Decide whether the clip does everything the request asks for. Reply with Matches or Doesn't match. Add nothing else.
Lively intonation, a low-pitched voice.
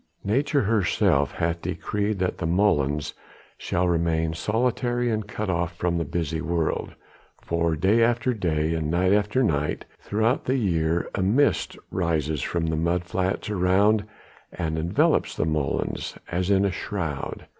Doesn't match